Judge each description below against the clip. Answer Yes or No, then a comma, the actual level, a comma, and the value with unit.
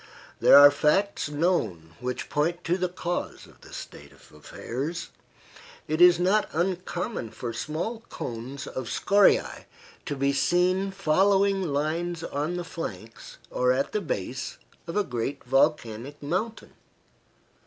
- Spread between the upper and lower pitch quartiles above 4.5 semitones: Yes, average, 5.1 semitones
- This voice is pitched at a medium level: Yes, medium, 160 Hz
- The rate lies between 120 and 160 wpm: Yes, slow, 135 wpm